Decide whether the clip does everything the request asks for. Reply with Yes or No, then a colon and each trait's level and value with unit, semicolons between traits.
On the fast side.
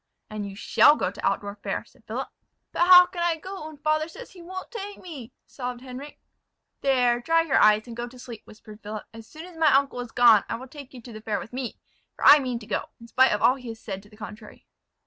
Yes: fast, 255 wpm